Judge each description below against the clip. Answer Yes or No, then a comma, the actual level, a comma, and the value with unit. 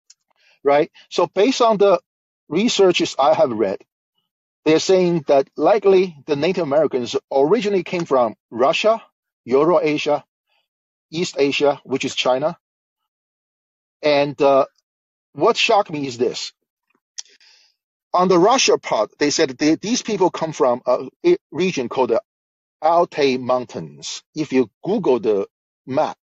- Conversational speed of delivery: No, slow, 125 wpm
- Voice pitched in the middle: Yes, medium, 155 Hz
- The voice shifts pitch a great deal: Yes, wide, 6.0 semitones